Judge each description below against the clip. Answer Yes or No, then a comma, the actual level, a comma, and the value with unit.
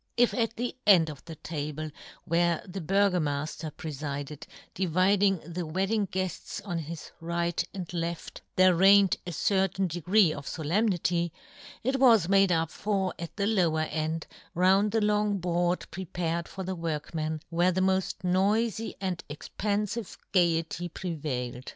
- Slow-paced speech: No, average, 150 wpm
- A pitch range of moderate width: Yes, average, 3.2 semitones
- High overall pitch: No, medium, 175 Hz